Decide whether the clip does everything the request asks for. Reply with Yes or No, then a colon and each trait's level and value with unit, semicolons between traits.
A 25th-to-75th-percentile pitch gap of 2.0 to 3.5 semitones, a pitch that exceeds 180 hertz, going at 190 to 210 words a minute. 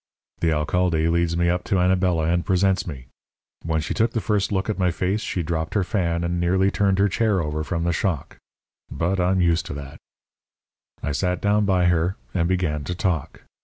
No: narrow, 2.4 semitones; very low, 90 Hz; average, 200 wpm